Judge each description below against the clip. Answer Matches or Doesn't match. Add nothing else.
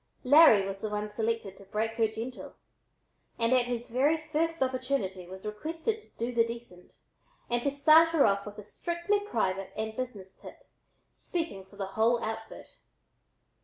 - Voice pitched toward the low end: Doesn't match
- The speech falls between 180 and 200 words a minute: Doesn't match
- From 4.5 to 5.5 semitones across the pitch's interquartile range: Matches